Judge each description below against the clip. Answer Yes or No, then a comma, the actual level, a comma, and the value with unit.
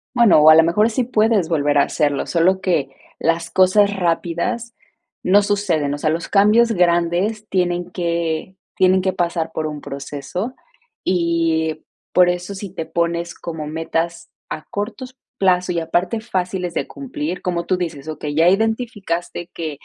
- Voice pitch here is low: No, medium, 175 Hz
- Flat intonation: No, average, 3.3 semitones